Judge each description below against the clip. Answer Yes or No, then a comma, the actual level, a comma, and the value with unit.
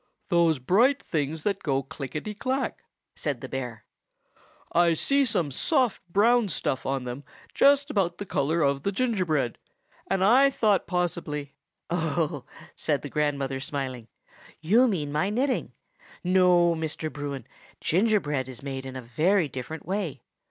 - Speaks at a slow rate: No, average, 145 wpm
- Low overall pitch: No, medium, 160 Hz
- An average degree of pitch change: No, wide, 6.3 semitones